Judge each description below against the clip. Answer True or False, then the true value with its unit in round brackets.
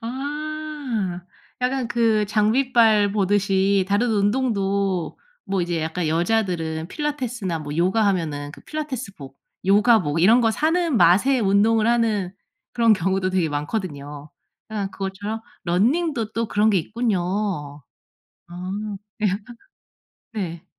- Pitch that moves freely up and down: False (4.5 semitones)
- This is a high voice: True (205 Hz)